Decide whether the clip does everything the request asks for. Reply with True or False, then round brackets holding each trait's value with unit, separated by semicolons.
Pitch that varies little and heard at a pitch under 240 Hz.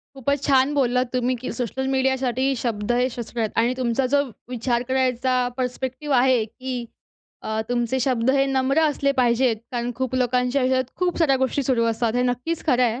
False (1.6 semitones; 255 Hz)